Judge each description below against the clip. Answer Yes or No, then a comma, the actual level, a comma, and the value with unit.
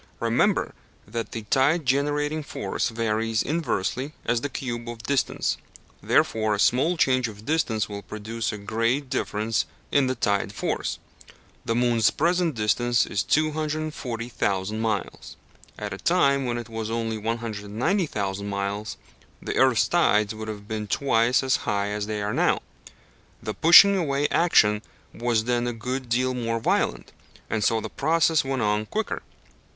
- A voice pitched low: Yes, low, 115 Hz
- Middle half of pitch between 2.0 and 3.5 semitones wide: No, average, 4.3 semitones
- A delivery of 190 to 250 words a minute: No, average, 155 wpm